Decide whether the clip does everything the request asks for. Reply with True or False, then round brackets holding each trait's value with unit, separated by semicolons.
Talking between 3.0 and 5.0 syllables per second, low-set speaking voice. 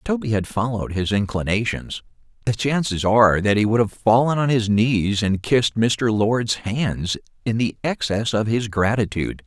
True (4.9 syllables/s; 110 Hz)